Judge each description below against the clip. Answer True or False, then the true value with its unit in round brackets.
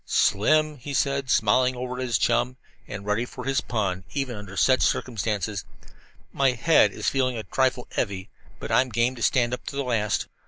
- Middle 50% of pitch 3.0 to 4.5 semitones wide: True (3.6 semitones)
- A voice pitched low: True (125 Hz)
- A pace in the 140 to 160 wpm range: False (190 wpm)